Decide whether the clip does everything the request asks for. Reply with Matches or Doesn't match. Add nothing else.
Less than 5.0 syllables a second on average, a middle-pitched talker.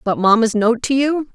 Doesn't match